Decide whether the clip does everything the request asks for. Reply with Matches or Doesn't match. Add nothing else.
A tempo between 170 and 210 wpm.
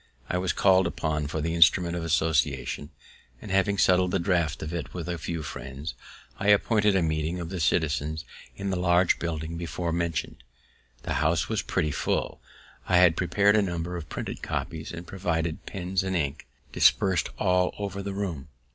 Matches